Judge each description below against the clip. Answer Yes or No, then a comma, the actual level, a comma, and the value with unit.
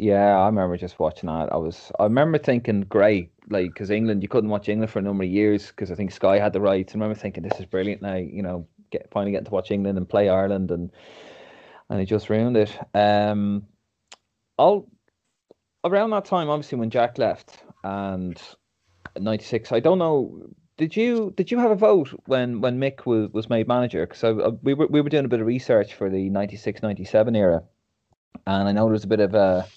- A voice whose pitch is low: Yes, low, 105 Hz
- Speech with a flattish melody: No, average, 3.3 semitones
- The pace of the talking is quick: Yes, fast, 220 wpm